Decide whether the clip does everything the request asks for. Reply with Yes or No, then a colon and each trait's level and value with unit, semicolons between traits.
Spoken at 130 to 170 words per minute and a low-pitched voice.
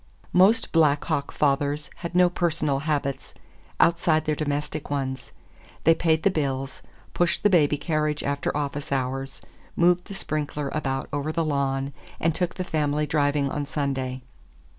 No: average, 150 wpm; medium, 150 Hz